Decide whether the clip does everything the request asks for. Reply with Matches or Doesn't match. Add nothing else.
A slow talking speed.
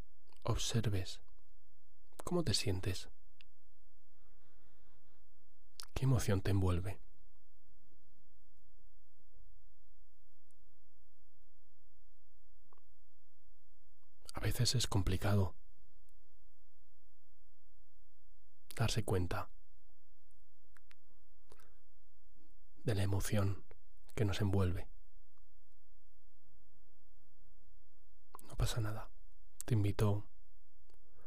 Matches